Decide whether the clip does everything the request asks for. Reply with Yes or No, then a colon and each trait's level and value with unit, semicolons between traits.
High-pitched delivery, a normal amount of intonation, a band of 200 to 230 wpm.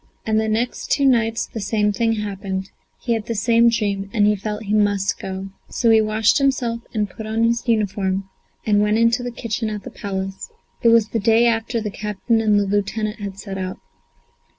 No: high, 215 Hz; narrow, 2.2 semitones; fast, 205 wpm